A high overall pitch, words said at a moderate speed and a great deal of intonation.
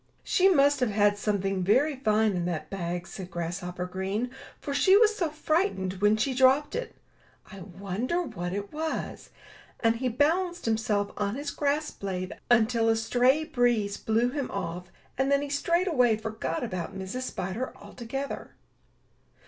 Yes: high, 225 Hz; average, 165 wpm; wide, 6.4 semitones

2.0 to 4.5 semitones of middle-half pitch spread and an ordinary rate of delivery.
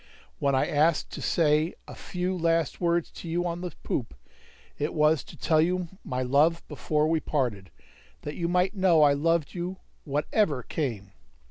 Yes: average, 3.2 semitones; average, 170 wpm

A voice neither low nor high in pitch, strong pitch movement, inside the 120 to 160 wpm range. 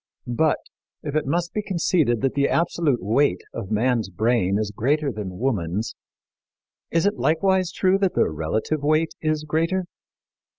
Yes: medium, 145 Hz; wide, 7.3 semitones; average, 155 wpm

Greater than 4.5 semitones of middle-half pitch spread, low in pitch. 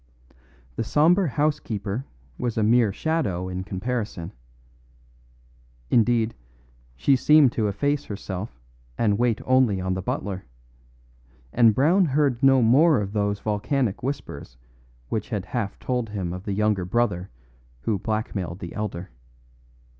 Yes: average, 4.9 semitones; low, 110 Hz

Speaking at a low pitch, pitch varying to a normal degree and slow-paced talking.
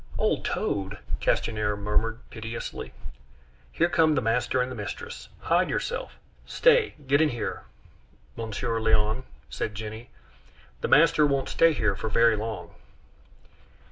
Yes: low, 115 Hz; average, 4.8 semitones; slow, 125 wpm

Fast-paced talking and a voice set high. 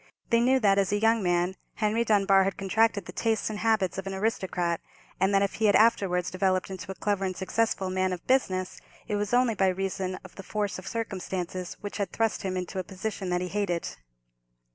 Yes: fast, 215 wpm; high, 195 Hz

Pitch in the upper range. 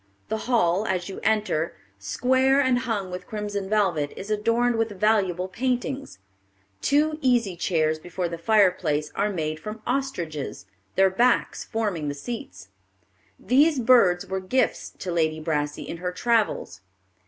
Yes: high, 200 Hz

